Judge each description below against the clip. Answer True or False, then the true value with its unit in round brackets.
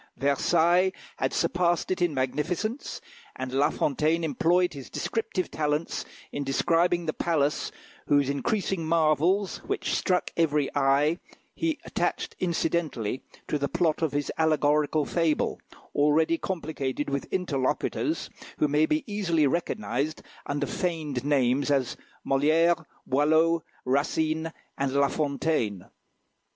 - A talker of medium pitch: True (155 Hz)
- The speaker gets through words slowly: True (120 wpm)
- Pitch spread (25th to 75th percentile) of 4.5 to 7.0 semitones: False (3.2 semitones)